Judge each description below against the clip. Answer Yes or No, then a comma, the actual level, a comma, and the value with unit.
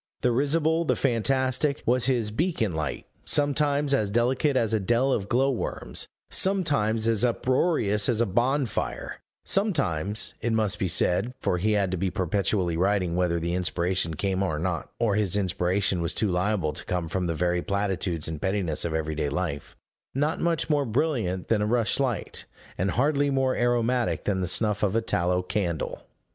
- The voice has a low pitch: Yes, low, 105 Hz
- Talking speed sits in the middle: Yes, average, 175 wpm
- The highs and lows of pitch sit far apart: Yes, wide, 6.1 semitones